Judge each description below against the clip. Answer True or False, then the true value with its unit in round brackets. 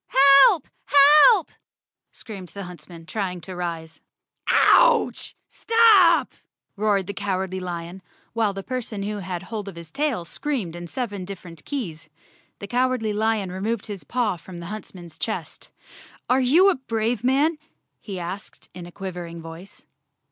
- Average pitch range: False (6.1 semitones)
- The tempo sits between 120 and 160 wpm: True (150 wpm)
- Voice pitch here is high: True (200 Hz)